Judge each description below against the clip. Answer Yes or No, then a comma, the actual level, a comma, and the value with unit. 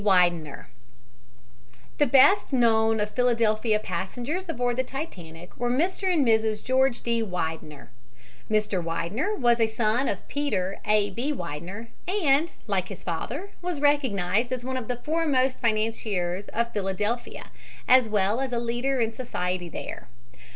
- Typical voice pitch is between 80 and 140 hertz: No, high, 230 Hz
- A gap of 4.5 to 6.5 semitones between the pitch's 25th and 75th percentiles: Yes, average, 4.8 semitones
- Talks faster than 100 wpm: Yes, average, 145 wpm